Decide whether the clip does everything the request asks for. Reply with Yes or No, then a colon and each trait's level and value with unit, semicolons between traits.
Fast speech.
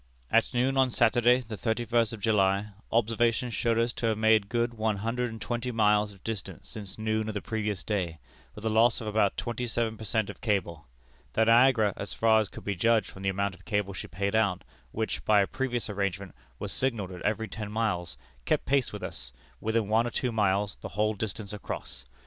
Yes: fast, 215 wpm